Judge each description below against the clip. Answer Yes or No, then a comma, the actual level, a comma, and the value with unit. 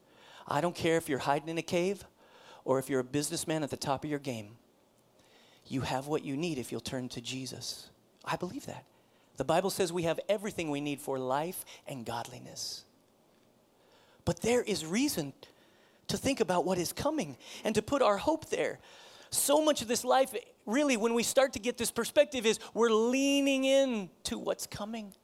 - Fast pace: No, average, 195 wpm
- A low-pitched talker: No, high, 190 Hz